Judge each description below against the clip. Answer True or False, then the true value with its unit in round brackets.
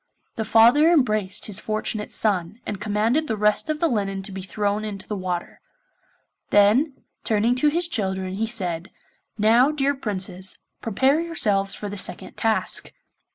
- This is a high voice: True (215 Hz)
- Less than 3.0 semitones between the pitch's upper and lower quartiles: False (4.1 semitones)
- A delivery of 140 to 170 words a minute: True (155 wpm)